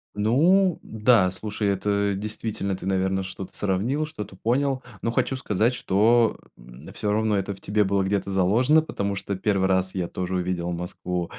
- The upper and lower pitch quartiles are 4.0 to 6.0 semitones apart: No, average, 3.0 semitones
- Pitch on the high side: No, low, 100 Hz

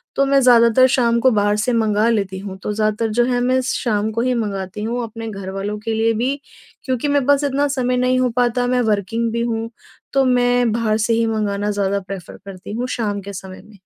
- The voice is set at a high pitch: Yes, high, 225 Hz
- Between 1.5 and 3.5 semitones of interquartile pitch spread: Yes, average, 3.1 semitones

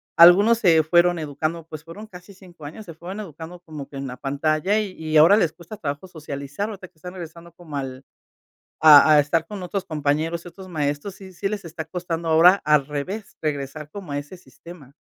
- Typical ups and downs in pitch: Yes, average, 3.5 semitones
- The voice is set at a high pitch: No, medium, 165 Hz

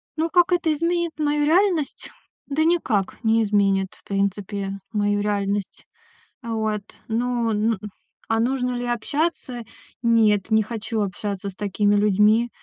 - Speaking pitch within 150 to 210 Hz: No, high, 225 Hz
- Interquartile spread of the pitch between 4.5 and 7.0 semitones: Yes, average, 4.8 semitones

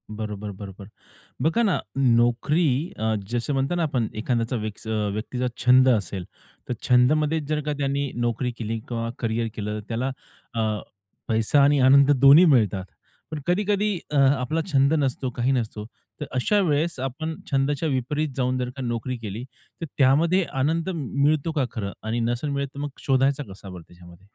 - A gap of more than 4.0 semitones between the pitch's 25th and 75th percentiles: Yes, average, 4.5 semitones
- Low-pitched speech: Yes, low, 130 Hz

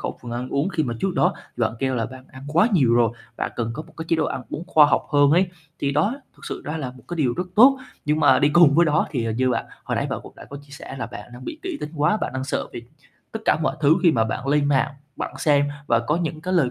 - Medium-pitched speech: Yes, medium, 145 Hz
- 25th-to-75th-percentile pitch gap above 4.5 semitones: No, average, 4.1 semitones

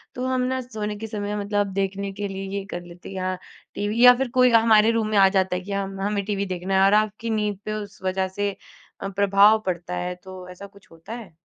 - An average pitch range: No, narrow, 2.1 semitones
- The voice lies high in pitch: Yes, high, 200 Hz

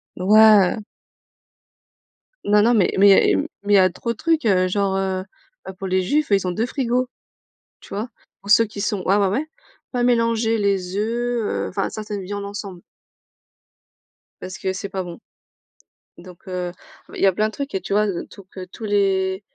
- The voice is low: No, high, 200 Hz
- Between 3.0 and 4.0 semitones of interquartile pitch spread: No, narrow, 2.6 semitones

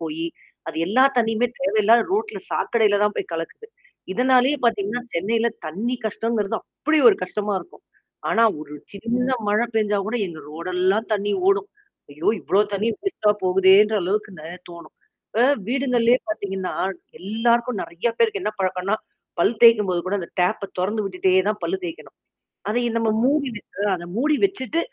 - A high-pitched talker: Yes, high, 215 Hz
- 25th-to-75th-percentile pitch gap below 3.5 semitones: No, average, 4.2 semitones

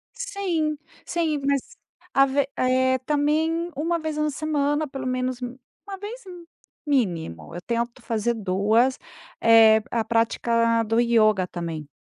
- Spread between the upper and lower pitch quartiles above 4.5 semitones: Yes, average, 5.1 semitones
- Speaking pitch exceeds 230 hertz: Yes, very high, 255 Hz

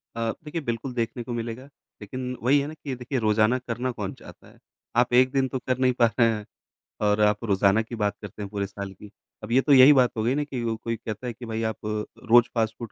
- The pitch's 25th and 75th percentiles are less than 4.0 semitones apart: Yes, average, 3.0 semitones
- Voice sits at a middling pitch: No, low, 115 Hz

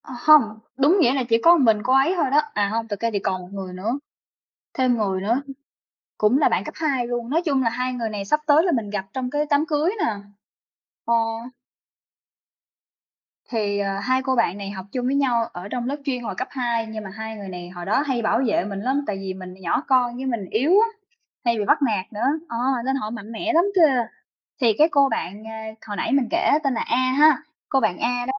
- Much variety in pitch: No, average, 4.6 semitones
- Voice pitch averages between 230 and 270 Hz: Yes, high, 235 Hz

